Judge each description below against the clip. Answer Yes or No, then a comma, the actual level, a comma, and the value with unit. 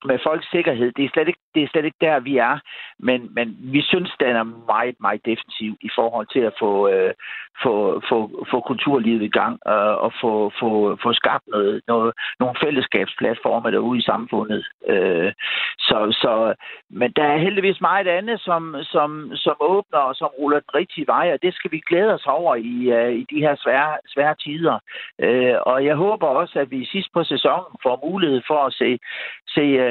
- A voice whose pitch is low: No, medium, 150 Hz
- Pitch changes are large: Yes, wide, 6.0 semitones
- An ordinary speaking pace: Yes, average, 200 wpm